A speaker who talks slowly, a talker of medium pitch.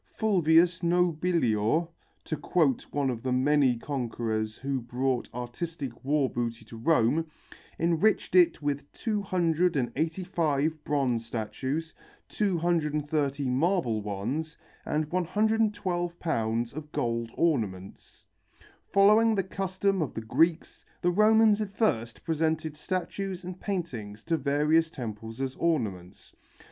Yes: slow, 110 wpm; medium, 155 Hz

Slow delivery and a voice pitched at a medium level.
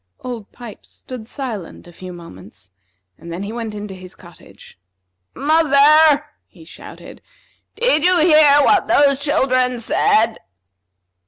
No: slow, 130 wpm; high, 245 Hz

